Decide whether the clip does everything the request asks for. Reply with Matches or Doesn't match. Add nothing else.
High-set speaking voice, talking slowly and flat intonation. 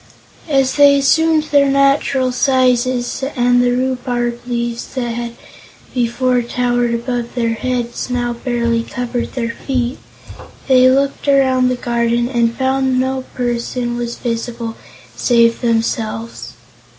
Matches